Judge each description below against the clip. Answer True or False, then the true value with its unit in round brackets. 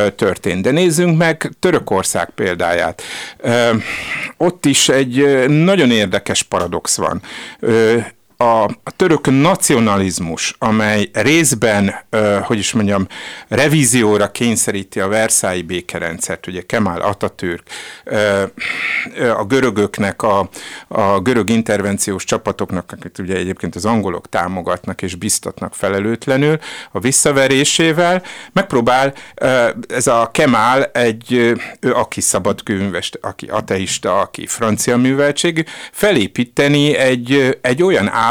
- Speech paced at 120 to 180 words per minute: False (110 wpm)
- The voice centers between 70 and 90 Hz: False (115 Hz)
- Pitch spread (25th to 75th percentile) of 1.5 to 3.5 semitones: False (5.6 semitones)